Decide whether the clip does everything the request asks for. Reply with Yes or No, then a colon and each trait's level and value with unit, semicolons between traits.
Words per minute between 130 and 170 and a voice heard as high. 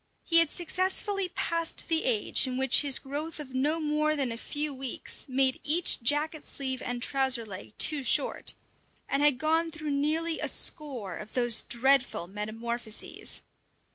Yes: average, 160 wpm; very high, 280 Hz